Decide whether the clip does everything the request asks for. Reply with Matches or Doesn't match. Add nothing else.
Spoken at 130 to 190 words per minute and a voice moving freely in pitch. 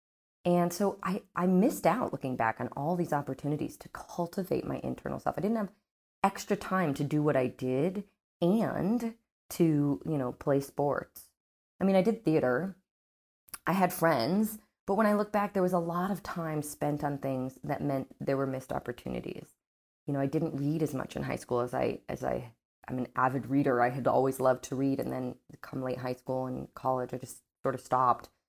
Doesn't match